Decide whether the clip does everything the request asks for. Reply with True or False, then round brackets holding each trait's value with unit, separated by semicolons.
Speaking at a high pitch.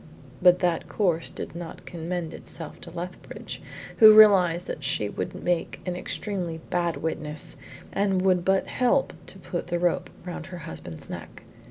False (175 Hz)